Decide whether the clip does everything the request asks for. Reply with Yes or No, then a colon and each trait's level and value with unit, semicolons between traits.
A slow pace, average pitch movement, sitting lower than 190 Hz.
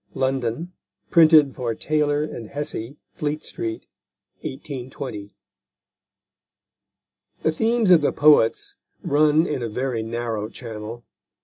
Yes: slow, 105 wpm; average, 4.8 semitones; low, 135 Hz